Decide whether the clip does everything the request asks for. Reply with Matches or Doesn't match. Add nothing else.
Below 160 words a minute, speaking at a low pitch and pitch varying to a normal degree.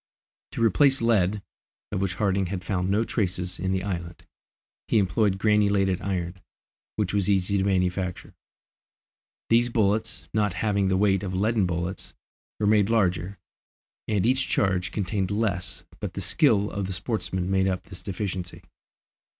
Doesn't match